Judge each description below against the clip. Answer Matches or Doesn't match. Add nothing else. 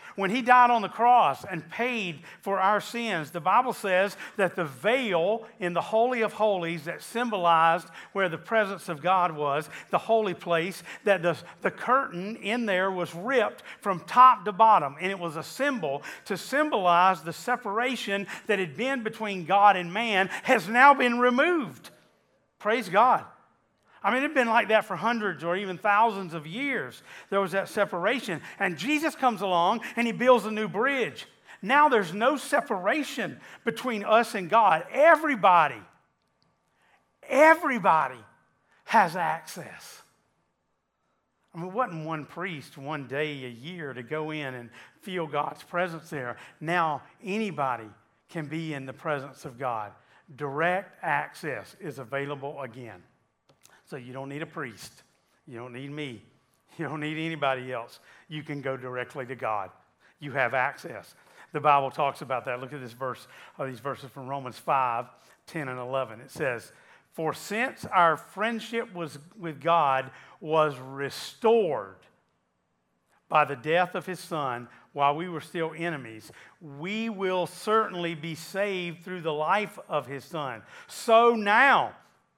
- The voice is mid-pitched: Matches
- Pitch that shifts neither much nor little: Doesn't match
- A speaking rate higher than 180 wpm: Doesn't match